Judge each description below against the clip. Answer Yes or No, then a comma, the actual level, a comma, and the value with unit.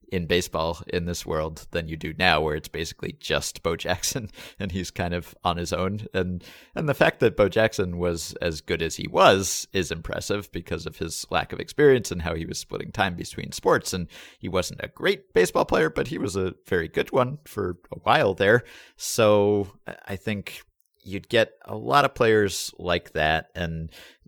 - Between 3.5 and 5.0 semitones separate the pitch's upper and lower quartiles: No, average, 2.9 semitones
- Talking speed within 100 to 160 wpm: No, average, 200 wpm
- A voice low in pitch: Yes, very low, 90 Hz